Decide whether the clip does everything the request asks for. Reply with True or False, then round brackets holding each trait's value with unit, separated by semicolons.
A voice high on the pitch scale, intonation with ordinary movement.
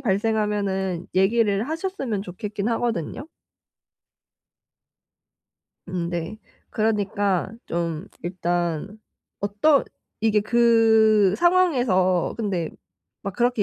True (205 Hz; 3.6 semitones)